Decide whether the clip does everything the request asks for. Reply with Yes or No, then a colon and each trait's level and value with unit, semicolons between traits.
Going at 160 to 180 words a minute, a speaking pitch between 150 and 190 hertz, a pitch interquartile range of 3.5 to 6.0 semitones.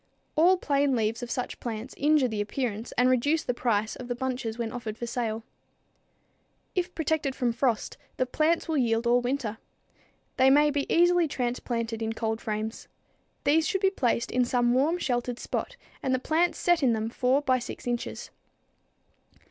No: average, 175 wpm; very high, 250 Hz; average, 3.9 semitones